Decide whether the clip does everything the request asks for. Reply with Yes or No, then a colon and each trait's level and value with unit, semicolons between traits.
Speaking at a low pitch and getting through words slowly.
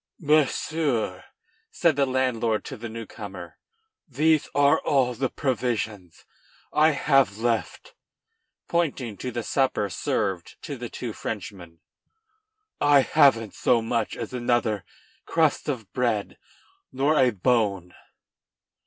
Yes: low, 120 Hz; slow, 120 wpm